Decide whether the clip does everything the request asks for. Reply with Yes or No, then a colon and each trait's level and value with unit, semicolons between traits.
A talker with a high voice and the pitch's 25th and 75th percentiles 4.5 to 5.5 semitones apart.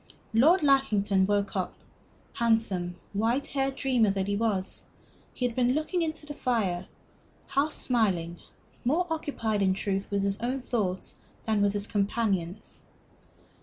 Yes: high, 220 Hz; average, 5.1 semitones